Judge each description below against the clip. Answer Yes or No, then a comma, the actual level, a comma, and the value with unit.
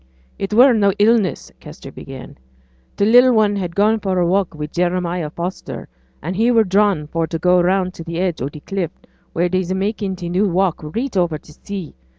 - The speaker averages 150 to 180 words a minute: No, average, 195 wpm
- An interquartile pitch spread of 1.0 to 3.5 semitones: Yes, average, 3.1 semitones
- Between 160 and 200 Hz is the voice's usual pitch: Yes, medium, 185 Hz